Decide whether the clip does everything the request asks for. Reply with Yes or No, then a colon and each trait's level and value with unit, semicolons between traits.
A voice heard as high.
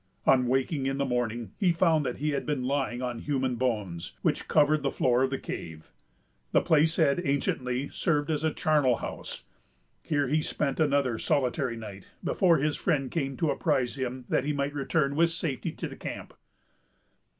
No: medium, 140 Hz